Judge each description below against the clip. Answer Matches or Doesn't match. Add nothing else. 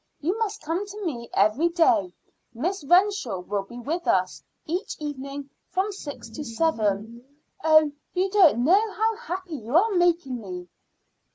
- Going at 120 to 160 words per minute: Matches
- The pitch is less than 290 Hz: Doesn't match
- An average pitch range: Doesn't match